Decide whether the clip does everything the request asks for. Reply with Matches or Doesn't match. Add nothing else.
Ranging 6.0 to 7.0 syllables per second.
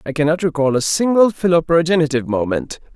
Matches